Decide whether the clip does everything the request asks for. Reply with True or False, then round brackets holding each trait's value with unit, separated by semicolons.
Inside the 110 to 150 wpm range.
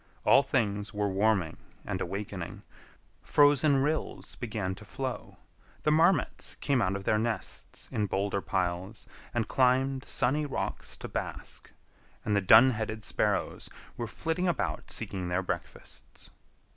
True (135 wpm)